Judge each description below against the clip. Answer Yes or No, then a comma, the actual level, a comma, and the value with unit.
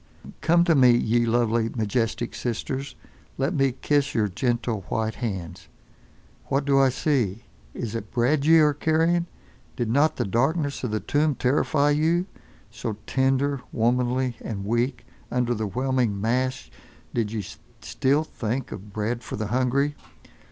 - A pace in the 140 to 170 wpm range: Yes, average, 145 wpm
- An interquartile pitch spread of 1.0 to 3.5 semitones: No, average, 3.9 semitones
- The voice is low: Yes, low, 125 Hz